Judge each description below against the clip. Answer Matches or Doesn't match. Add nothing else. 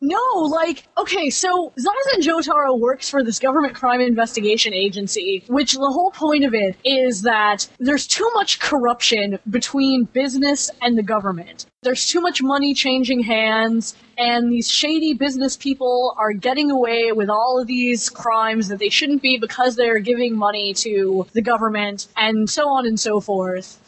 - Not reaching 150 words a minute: Doesn't match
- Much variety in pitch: Doesn't match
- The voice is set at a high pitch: Matches